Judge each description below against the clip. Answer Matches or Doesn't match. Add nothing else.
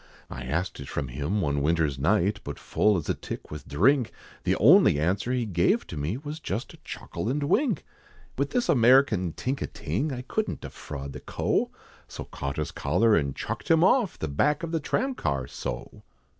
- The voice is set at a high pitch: Doesn't match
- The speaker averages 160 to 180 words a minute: Doesn't match